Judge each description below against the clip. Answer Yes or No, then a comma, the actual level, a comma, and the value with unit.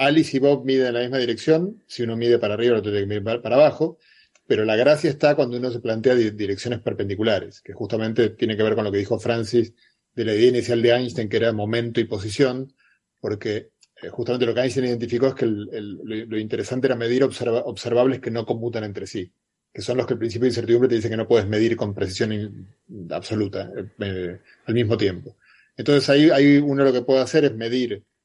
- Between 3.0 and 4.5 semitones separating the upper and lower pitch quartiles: No, narrow, 2.6 semitones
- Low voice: Yes, low, 120 Hz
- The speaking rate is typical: No, fast, 220 wpm